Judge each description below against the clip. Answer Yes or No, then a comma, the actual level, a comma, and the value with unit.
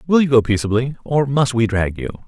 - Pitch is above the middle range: No, low, 125 Hz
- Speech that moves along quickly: Yes, fast, 235 wpm